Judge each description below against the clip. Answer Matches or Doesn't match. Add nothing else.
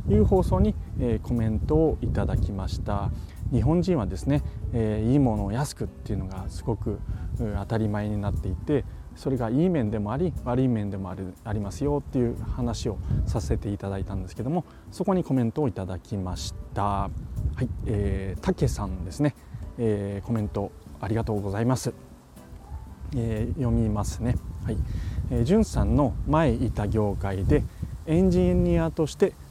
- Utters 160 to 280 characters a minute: Doesn't match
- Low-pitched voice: Matches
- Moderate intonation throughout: Matches